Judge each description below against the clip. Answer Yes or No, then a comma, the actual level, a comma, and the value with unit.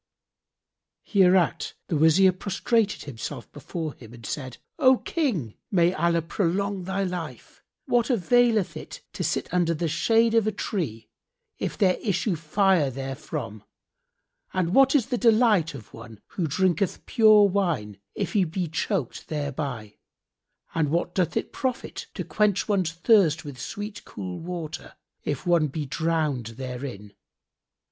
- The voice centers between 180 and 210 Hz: No, medium, 170 Hz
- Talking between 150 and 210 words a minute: No, average, 140 wpm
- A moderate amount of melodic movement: No, wide, 5.8 semitones